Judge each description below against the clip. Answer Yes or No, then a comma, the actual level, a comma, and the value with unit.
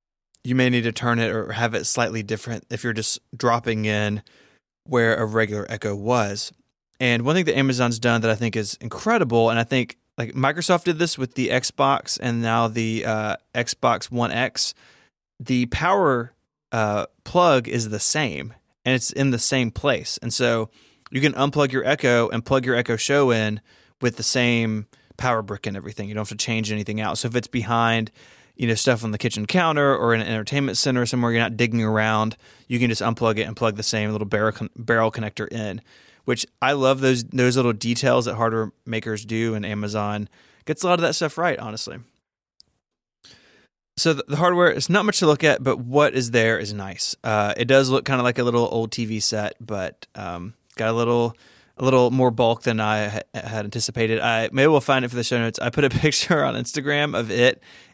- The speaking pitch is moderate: No, low, 115 Hz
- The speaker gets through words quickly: Yes, fast, 210 wpm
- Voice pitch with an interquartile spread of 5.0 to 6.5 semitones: No, average, 2.9 semitones